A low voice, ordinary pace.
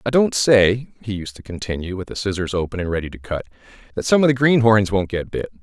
No: low, 105 Hz; fast, 245 wpm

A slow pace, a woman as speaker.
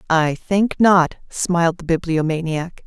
Yes: slow, 125 wpm; female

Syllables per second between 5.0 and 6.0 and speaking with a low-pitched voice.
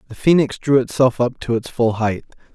Yes: 5.4 syllables/s; low, 125 Hz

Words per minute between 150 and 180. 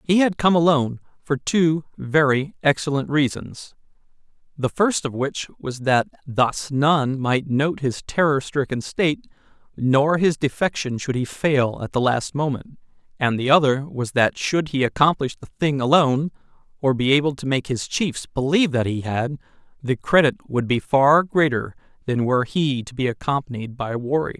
Yes: average, 170 wpm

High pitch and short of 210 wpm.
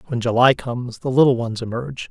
No: low, 125 Hz; average, 200 wpm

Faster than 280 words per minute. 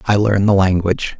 No: average, 200 wpm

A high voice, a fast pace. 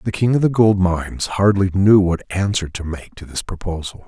No: very low, 95 Hz; fast, 220 wpm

